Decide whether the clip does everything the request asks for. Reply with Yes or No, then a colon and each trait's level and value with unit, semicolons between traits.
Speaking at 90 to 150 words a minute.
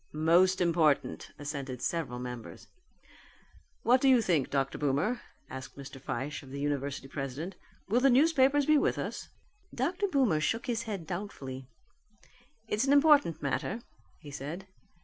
Yes: average, 145 wpm